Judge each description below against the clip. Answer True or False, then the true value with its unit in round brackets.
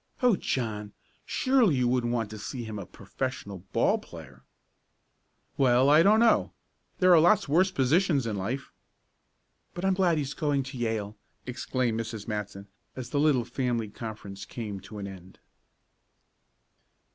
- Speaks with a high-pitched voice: False (125 Hz)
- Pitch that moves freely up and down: True (5.9 semitones)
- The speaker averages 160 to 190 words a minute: False (150 wpm)